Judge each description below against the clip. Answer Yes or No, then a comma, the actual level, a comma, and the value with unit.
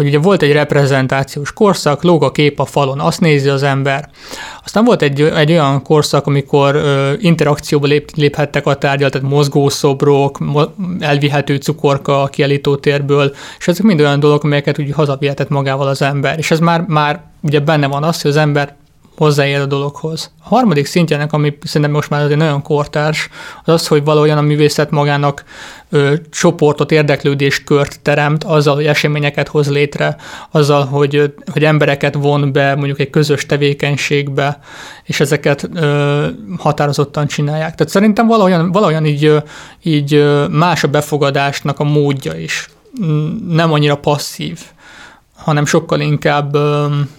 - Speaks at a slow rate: No, average, 150 wpm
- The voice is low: No, medium, 145 Hz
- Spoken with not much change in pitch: Yes, narrow, 1.3 semitones